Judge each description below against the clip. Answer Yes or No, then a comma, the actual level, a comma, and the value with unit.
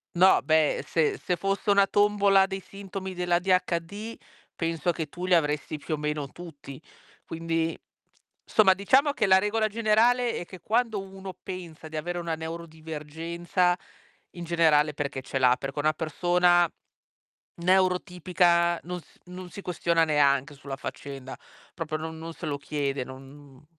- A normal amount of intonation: Yes, average, 3.6 semitones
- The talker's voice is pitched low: No, medium, 170 Hz